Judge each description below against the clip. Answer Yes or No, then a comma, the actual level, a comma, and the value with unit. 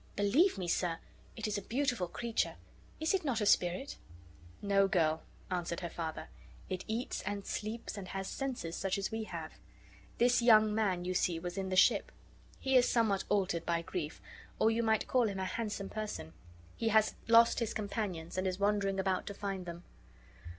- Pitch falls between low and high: No, high, 200 Hz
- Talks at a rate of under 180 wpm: No, average, 185 wpm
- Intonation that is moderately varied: Yes, average, 3.6 semitones